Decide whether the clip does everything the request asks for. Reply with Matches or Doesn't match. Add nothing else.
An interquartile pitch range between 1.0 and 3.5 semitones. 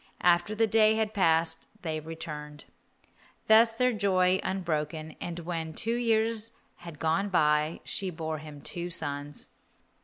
Doesn't match